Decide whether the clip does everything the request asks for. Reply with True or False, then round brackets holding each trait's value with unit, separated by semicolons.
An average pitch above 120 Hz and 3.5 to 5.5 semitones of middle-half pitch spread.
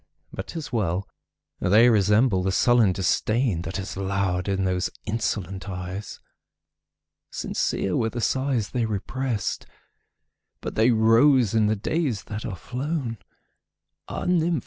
False (110 Hz; 4.3 semitones)